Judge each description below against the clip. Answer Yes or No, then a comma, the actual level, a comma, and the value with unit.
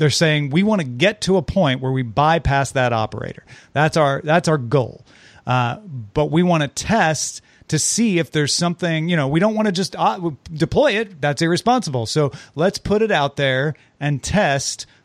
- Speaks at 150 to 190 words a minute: No, average, 200 wpm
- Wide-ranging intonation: No, average, 4.4 semitones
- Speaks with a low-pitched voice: No, medium, 150 Hz